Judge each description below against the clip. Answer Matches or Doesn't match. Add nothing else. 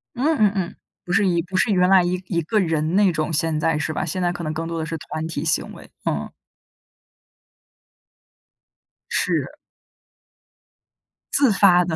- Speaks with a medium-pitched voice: Matches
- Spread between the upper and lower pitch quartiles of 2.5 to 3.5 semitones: Matches